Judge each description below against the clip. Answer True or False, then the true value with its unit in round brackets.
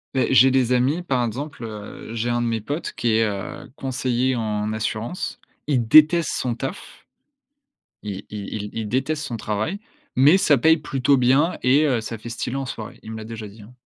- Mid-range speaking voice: False (120 Hz)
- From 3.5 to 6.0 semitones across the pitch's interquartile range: True (3.8 semitones)